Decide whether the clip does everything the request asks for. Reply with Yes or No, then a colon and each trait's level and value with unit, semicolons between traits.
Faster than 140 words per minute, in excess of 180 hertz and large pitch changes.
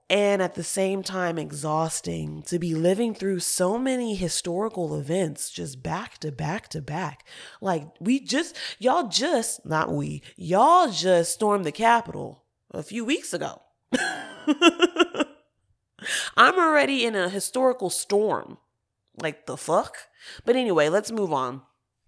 No: slow, 135 wpm; high, 190 Hz; wide, 6.8 semitones